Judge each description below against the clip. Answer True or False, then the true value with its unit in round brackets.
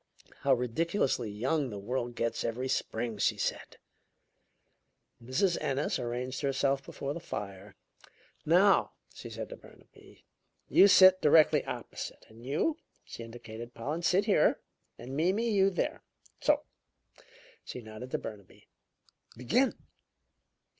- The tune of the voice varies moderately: False (6.3 semitones)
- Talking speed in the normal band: False (125 wpm)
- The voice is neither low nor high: False (130 Hz)